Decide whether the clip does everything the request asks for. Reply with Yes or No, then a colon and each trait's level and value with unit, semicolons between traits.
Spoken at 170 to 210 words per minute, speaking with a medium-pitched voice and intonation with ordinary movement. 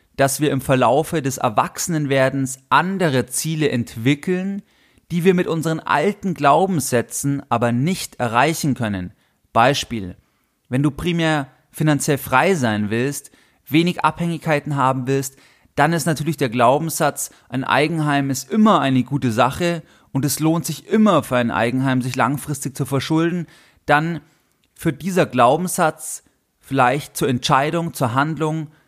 No: average, 135 wpm; medium, 145 Hz; average, 3.6 semitones